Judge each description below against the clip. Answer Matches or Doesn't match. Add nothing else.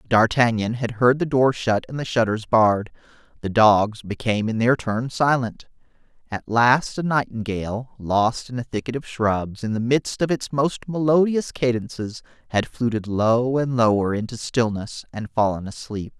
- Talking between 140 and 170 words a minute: Matches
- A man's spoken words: Matches